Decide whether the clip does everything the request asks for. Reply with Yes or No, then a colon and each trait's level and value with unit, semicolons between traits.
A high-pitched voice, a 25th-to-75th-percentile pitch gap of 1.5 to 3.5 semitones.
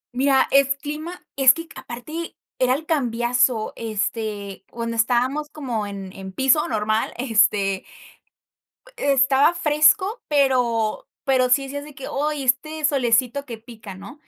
No: very high, 255 Hz; average, 4.1 semitones